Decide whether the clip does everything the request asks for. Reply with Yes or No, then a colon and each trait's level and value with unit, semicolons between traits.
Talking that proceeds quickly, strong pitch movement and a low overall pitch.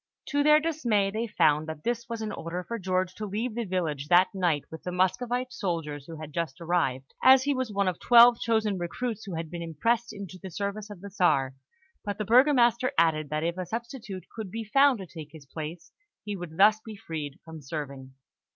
No: fast, 215 wpm; wide, 6.0 semitones; high, 190 Hz